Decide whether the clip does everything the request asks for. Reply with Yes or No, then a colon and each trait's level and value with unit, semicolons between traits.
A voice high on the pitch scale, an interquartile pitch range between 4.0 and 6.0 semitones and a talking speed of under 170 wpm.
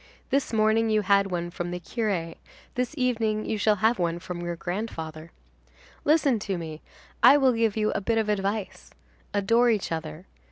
No: high, 210 Hz; average, 4.4 semitones; average, 175 wpm